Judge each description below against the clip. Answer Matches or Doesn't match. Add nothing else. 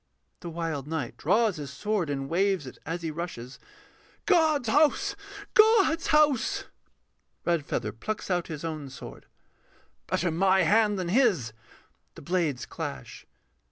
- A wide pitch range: Matches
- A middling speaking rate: Doesn't match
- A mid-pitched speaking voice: Matches